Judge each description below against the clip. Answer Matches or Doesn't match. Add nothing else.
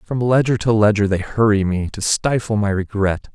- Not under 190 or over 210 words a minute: Matches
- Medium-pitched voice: Doesn't match